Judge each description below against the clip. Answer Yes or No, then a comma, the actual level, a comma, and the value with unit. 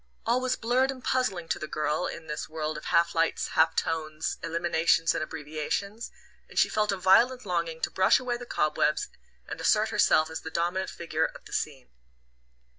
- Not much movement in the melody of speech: No, average, 4.9 semitones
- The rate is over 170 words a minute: Yes, average, 190 wpm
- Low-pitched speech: No, medium, 170 Hz